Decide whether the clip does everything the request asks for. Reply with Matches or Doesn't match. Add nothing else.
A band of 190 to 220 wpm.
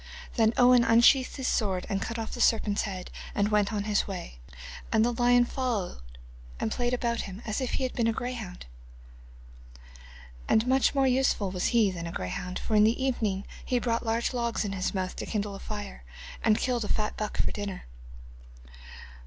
Matches